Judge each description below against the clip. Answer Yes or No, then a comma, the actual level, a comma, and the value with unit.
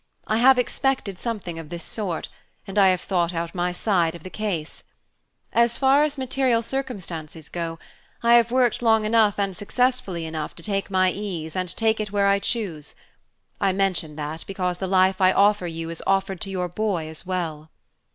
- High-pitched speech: Yes, high, 195 Hz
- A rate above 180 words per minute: Yes, average, 190 wpm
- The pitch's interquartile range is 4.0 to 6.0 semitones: Yes, average, 4.3 semitones